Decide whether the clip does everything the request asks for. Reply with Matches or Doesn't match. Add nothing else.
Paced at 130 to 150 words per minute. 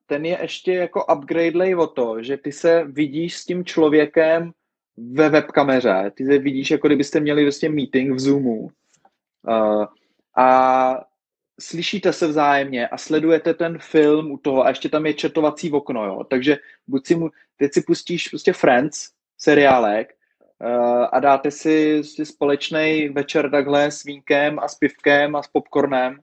Doesn't match